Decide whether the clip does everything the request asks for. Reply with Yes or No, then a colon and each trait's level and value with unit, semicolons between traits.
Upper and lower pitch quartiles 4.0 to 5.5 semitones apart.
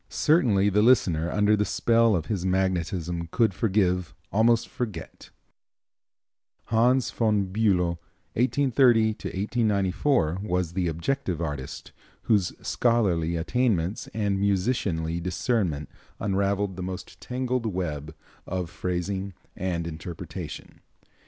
Yes: average, 4.4 semitones